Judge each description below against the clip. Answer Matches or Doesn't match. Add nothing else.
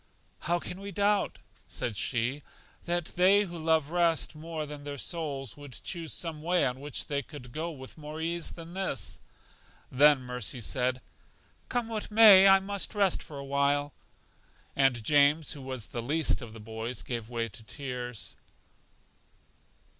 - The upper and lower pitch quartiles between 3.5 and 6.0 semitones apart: Matches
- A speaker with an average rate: Matches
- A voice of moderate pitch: Matches